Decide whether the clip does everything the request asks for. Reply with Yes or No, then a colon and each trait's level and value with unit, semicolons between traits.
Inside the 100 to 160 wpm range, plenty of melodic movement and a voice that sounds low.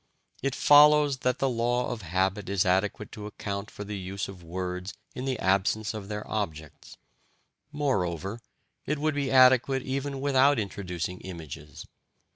Yes: average, 150 wpm; wide, 6.0 semitones; low, 105 Hz